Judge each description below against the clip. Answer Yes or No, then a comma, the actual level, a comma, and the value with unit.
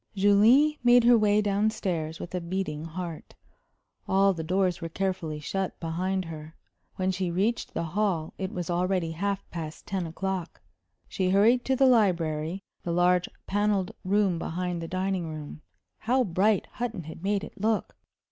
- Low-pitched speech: No, medium, 185 Hz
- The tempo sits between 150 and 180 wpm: Yes, average, 165 wpm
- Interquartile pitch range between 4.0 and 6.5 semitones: No, average, 3.4 semitones